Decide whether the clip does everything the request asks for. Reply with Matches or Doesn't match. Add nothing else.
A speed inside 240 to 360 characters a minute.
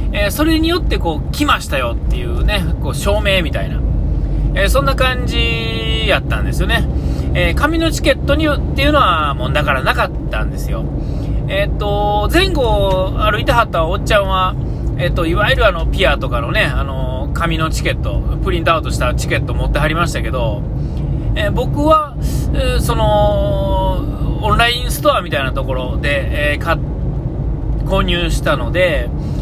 Matches